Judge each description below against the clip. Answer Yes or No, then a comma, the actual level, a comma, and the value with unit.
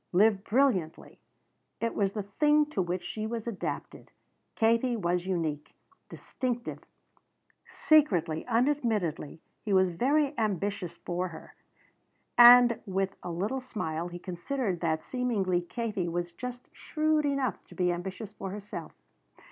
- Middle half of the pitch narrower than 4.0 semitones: No, wide, 5.6 semitones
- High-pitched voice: Yes, high, 200 Hz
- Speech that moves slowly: Yes, slow, 130 wpm